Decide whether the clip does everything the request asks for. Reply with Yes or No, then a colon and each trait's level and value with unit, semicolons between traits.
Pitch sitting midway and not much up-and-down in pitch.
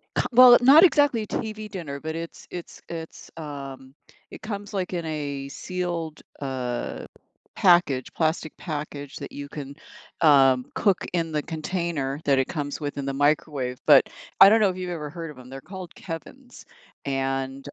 No: medium, 155 Hz; average, 4.7 semitones